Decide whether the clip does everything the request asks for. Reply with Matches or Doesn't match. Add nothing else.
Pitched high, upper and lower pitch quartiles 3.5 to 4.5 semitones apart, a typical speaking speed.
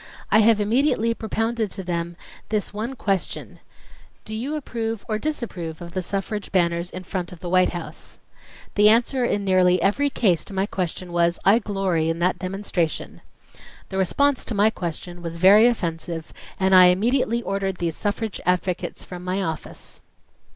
Matches